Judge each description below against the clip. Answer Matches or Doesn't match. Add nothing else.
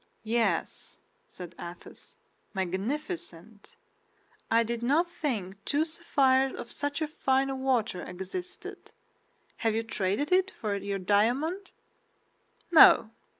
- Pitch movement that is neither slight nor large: Doesn't match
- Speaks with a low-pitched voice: Doesn't match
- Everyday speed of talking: Doesn't match